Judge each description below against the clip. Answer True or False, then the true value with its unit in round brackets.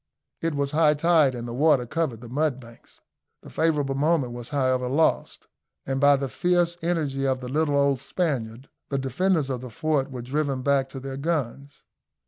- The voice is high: False (140 Hz)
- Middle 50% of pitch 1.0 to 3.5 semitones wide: True (3.2 semitones)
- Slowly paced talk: False (180 wpm)